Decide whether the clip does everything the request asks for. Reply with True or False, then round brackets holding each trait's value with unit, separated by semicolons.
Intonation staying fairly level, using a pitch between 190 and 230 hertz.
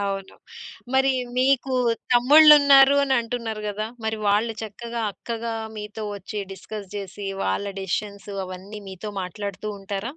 False (3.2 semitones; 215 Hz)